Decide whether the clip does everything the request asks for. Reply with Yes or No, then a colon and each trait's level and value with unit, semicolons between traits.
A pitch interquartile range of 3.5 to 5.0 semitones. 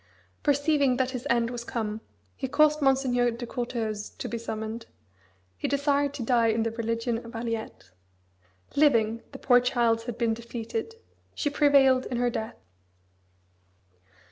No: average, 2.9 semitones